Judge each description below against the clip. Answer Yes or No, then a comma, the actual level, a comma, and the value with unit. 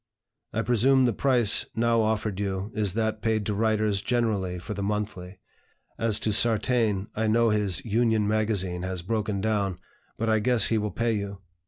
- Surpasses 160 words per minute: Yes, average, 175 wpm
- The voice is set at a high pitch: No, low, 110 Hz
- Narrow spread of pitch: Yes, narrow, 2.2 semitones